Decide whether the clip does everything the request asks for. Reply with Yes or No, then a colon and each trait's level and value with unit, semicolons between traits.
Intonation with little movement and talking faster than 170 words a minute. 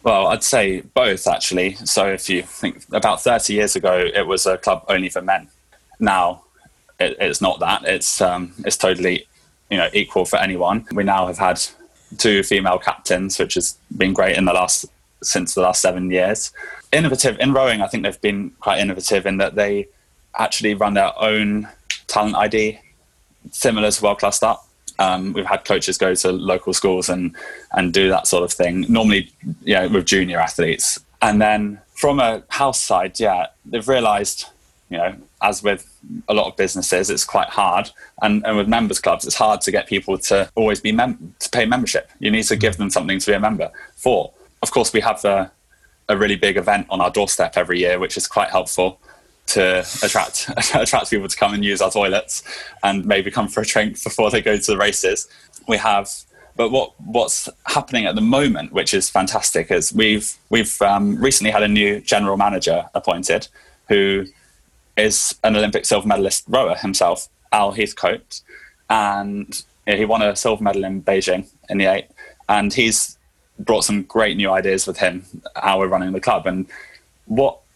Yes: narrow, 2.2 semitones; average, 190 wpm